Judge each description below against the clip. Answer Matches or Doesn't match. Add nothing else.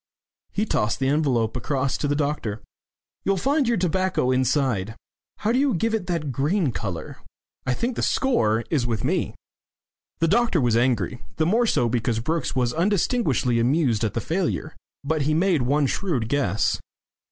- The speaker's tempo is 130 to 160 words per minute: Doesn't match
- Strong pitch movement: Matches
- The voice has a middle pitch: Matches